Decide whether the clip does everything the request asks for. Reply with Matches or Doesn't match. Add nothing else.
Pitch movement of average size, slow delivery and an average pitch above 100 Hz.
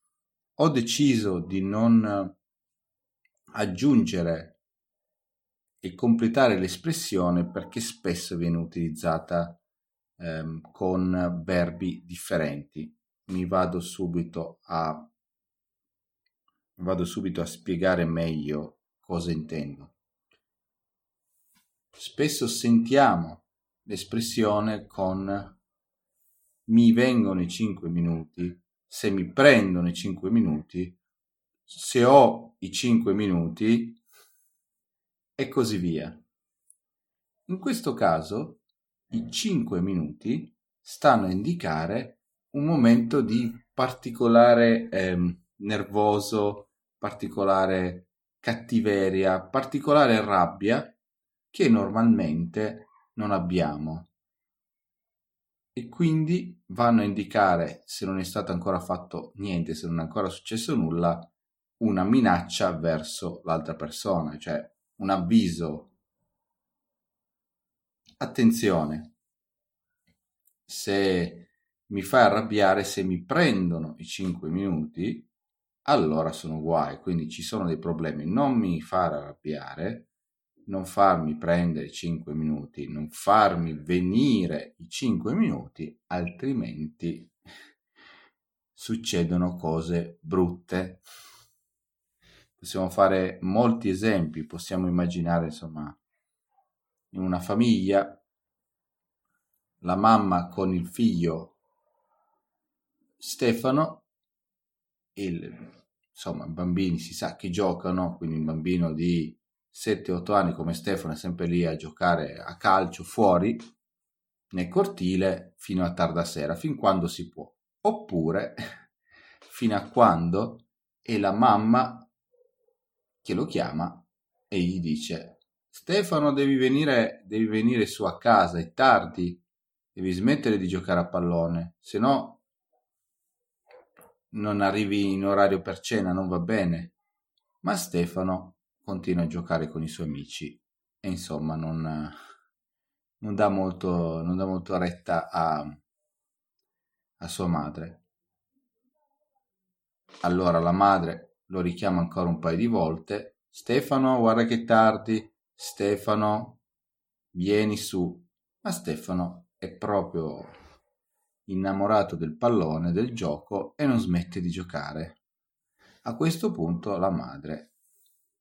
Doesn't match